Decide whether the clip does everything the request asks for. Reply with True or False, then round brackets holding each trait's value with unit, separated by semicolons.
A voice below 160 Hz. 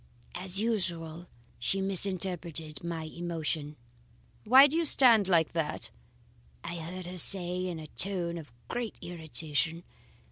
False (175 Hz)